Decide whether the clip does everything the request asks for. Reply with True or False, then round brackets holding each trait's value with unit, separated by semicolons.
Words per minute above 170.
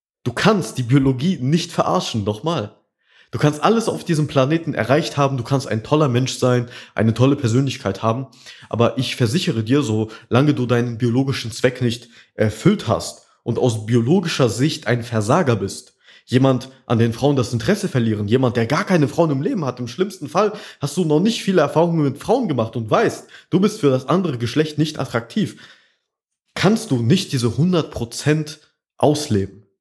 True (180 wpm)